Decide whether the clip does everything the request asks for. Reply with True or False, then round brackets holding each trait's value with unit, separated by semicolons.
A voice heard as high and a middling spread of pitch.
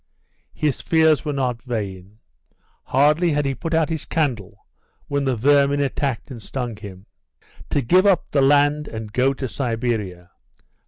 False (135 Hz; 4.4 semitones)